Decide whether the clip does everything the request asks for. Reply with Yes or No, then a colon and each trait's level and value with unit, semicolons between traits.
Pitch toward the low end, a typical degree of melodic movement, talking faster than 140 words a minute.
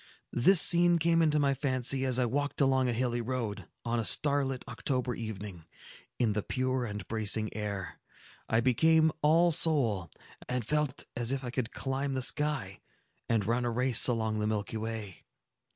Yes: low, 125 Hz; average, 4.0 semitones; average, 170 wpm